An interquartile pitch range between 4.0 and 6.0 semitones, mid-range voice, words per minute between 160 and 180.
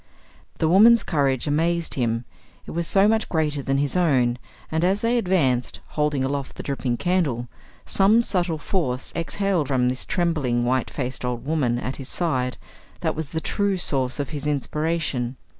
Yes: average, 5.1 semitones; medium, 150 Hz; average, 170 wpm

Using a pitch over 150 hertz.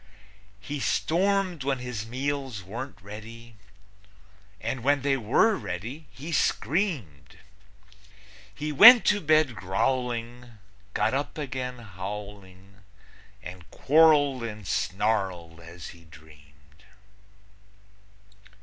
No: low, 115 Hz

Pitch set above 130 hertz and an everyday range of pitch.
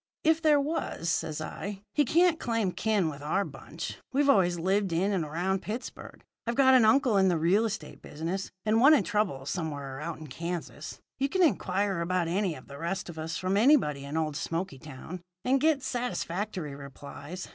No: high, 190 Hz; wide, 6.1 semitones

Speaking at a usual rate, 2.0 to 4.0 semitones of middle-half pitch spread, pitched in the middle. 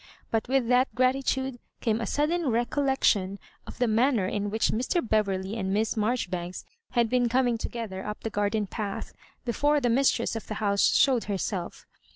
No: average, 180 wpm; average, 3.7 semitones; high, 230 Hz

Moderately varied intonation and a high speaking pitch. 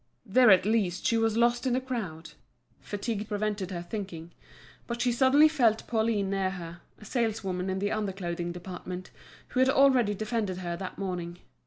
Yes: average, 4.2 semitones; high, 205 Hz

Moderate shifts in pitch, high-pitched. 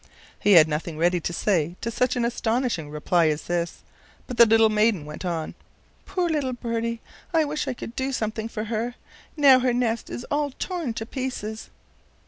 No: wide, 6.2 semitones; high, 225 Hz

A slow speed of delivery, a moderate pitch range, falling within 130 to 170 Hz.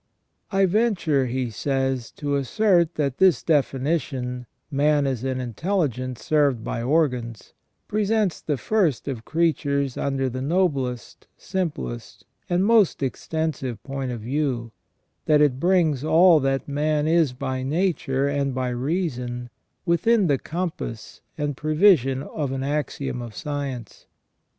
Yes: slow, 130 wpm; average, 4.2 semitones; medium, 140 Hz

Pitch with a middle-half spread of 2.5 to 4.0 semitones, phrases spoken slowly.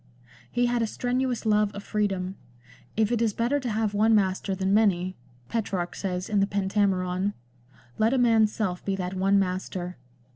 No: average, 2.9 semitones; average, 175 wpm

